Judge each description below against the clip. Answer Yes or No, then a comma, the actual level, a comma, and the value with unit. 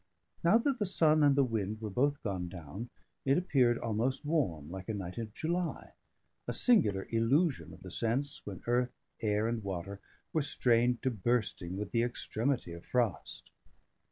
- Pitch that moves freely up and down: Yes, wide, 5.8 semitones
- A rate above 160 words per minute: Yes, average, 170 wpm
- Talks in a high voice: No, low, 115 Hz